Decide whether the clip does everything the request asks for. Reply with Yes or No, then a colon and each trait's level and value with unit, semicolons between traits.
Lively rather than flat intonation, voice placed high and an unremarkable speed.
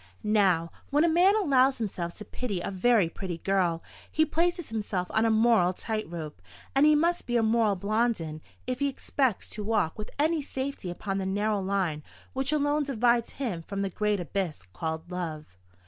Yes: wide, 6.5 semitones; high, 215 Hz; average, 185 wpm